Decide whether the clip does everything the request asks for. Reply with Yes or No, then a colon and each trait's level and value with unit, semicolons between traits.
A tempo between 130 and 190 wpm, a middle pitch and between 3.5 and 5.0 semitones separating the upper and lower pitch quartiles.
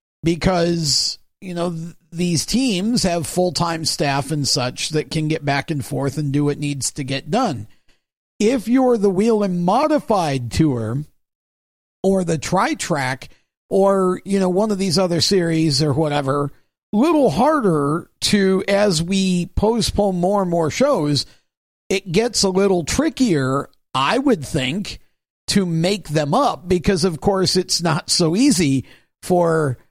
Yes: average, 155 wpm; medium, 175 Hz; average, 4.7 semitones